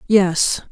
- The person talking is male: No, female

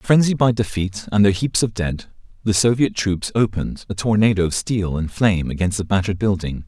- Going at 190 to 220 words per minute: Yes, average, 200 wpm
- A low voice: Yes, low, 100 Hz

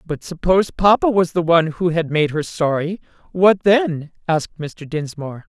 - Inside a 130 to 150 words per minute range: No, average, 175 wpm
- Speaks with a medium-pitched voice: Yes, medium, 170 Hz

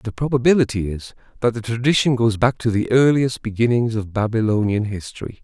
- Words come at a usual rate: Yes, average, 165 wpm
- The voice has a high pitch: No, low, 115 Hz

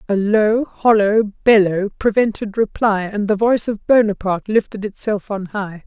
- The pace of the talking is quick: No, average, 155 wpm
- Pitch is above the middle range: Yes, high, 210 Hz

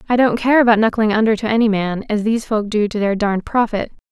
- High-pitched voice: Yes, high, 220 Hz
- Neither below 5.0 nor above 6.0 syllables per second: No, 6.5 syllables/s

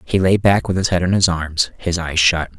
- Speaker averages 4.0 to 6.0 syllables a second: Yes, 5.0 syllables/s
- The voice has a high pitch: No, very low, 85 Hz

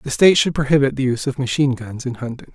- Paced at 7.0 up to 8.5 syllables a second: Yes, 7.2 syllables/s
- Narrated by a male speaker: Yes, male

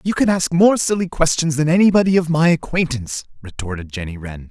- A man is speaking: Yes, male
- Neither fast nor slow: Yes, average, 185 wpm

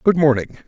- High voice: No, medium, 145 Hz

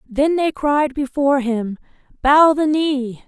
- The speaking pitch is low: No, very high, 280 Hz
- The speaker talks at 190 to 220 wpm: No, average, 145 wpm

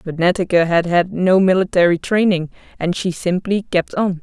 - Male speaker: No, female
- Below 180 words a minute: Yes, average, 170 wpm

